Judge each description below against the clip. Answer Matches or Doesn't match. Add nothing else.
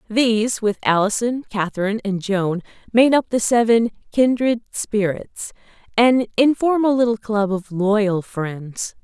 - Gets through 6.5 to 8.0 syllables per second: Doesn't match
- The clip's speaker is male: Doesn't match